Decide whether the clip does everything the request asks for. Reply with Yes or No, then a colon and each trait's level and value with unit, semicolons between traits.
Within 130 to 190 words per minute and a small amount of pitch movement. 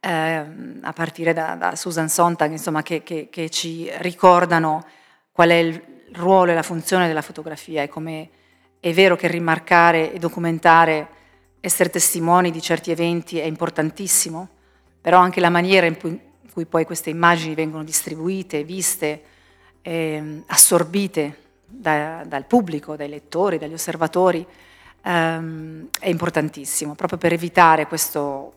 Yes: average, 140 wpm; narrow, 1.8 semitones